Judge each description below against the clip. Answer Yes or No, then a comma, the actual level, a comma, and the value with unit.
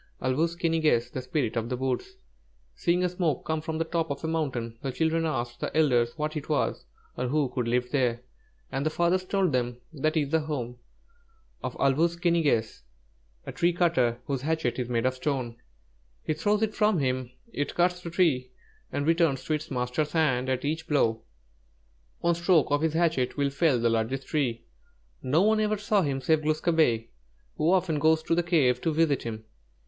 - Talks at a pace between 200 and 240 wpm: Yes, fast, 205 wpm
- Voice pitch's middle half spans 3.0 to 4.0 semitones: No, average, 4.6 semitones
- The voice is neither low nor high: Yes, medium, 150 Hz